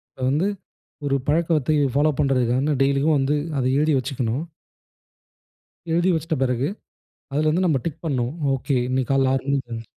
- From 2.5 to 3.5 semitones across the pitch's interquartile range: Yes, average, 2.9 semitones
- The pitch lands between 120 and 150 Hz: Yes, medium, 140 Hz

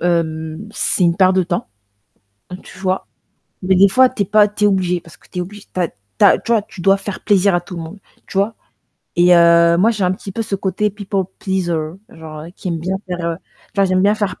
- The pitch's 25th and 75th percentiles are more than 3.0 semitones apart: No, narrow, 2.6 semitones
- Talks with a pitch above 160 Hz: Yes, medium, 185 Hz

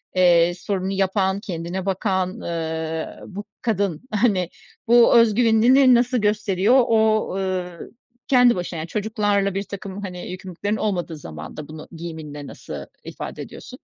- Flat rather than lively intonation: No, average, 3.7 semitones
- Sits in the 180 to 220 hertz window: Yes, high, 190 Hz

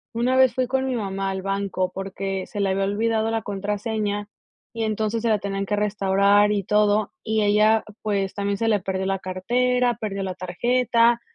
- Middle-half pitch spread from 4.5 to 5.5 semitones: No, narrow, 2.5 semitones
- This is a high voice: Yes, high, 205 Hz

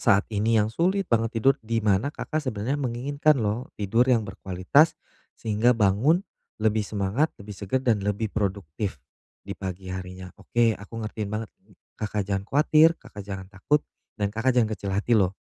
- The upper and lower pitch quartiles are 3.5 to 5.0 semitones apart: Yes, average, 3.8 semitones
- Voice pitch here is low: Yes, low, 110 Hz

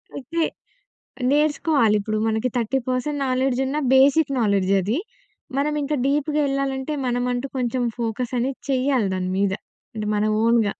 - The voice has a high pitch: Yes, very high, 255 Hz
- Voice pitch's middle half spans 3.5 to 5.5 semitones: Yes, average, 3.8 semitones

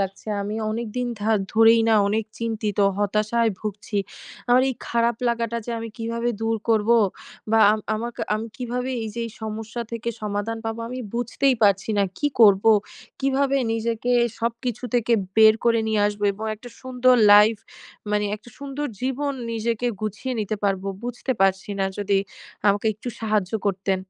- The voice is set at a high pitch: Yes, high, 225 Hz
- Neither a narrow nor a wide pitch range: No, narrow, 2.3 semitones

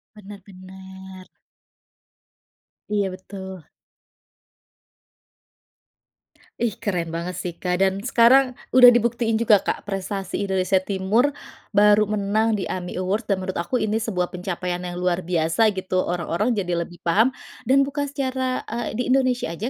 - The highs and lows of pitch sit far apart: No, average, 3.7 semitones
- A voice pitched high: Yes, high, 195 Hz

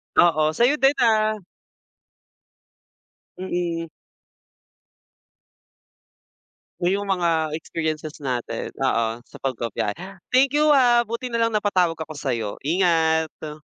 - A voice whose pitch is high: No, medium, 165 Hz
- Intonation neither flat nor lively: No, wide, 6.2 semitones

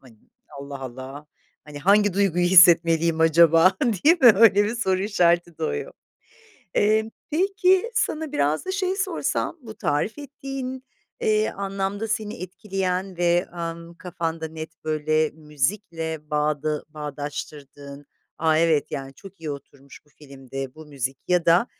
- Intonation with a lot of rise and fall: Yes, wide, 5.9 semitones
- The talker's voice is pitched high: No, medium, 170 Hz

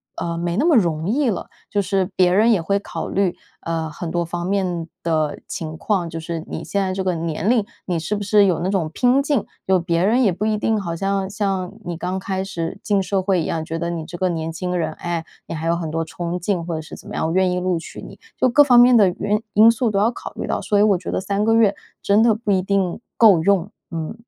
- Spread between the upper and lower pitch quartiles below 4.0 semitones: Yes, average, 3.4 semitones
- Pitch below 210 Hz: Yes, medium, 185 Hz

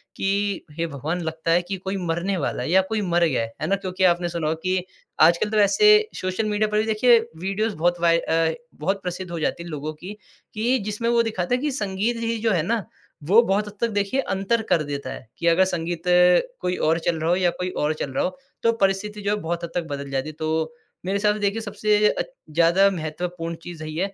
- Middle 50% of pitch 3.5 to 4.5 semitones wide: Yes, average, 3.9 semitones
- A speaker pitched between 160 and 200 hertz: Yes, medium, 185 Hz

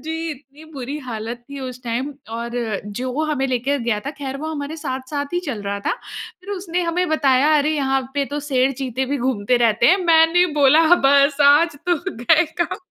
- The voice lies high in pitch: Yes, very high, 275 Hz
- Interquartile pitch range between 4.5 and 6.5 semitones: No, average, 3.8 semitones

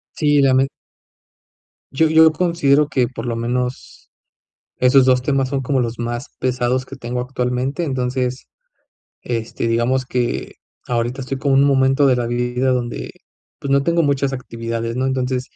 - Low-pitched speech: Yes, low, 130 Hz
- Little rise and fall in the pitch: Yes, narrow, 1.9 semitones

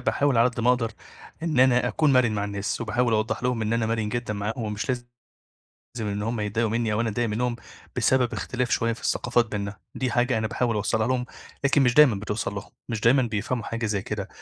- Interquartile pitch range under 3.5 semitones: Yes, narrow, 2.5 semitones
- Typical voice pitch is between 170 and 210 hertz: No, low, 115 Hz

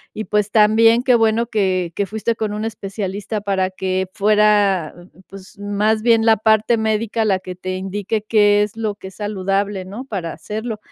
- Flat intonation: Yes, narrow, 2.1 semitones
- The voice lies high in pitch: Yes, high, 210 Hz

